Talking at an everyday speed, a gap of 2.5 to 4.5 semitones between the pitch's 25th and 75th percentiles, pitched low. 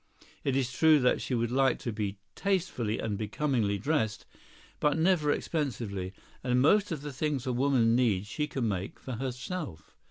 No: average, 170 wpm; average, 5.2 semitones; low, 125 Hz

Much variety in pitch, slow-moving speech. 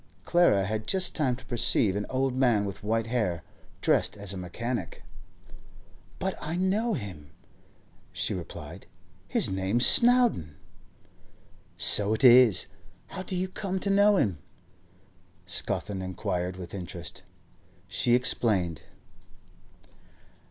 Yes: wide, 8.5 semitones; slow, 120 wpm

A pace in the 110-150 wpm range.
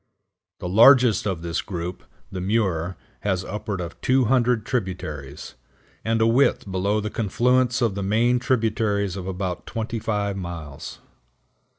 Yes: slow, 135 wpm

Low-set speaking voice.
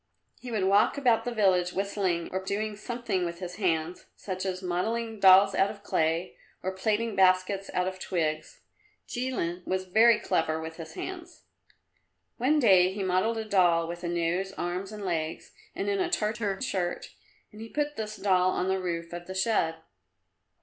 No: high, 190 Hz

